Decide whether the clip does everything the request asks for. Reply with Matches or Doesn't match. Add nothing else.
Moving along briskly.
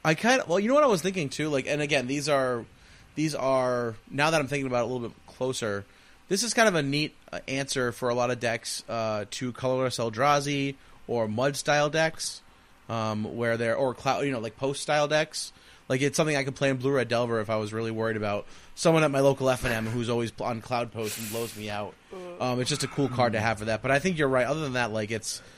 Matches